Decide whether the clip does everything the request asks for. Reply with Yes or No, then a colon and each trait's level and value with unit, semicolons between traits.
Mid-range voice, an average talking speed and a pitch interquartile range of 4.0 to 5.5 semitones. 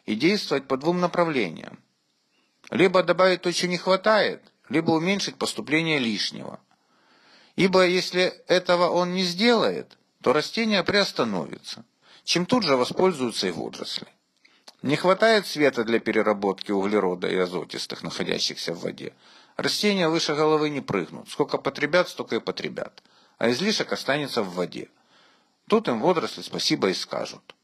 Yes: medium, 175 Hz; average, 135 wpm; average, 5.1 semitones